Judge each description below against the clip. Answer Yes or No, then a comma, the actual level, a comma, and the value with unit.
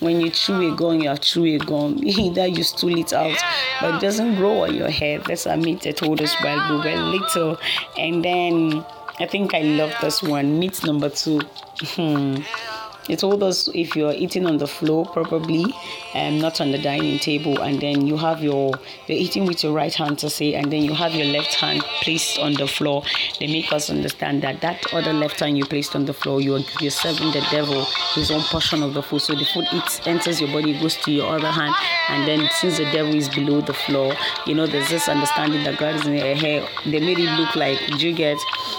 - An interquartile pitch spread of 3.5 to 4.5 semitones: No, narrow, 2.4 semitones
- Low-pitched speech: No, medium, 155 Hz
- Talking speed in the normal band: No, fast, 230 wpm